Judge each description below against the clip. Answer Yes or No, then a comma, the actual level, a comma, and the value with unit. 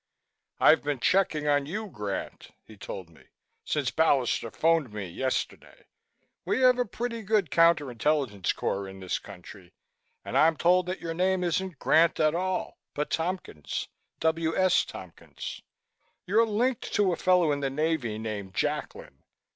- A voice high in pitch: No, medium, 160 Hz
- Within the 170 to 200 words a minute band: No, average, 155 wpm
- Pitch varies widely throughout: Yes, wide, 7.7 semitones